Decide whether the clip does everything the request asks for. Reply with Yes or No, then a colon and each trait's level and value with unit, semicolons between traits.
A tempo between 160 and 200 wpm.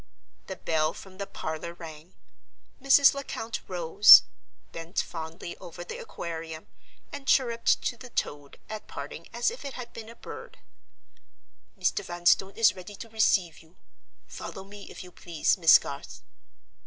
No: average, 150 wpm